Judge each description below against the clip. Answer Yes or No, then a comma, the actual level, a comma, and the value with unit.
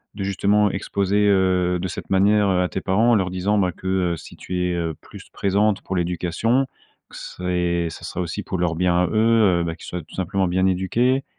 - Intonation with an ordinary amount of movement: No, narrow, 2.3 semitones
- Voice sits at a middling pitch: No, very low, 95 Hz